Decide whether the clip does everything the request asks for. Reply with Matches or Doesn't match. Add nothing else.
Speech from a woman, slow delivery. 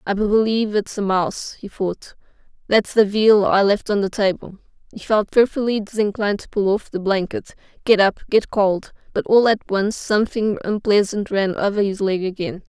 Doesn't match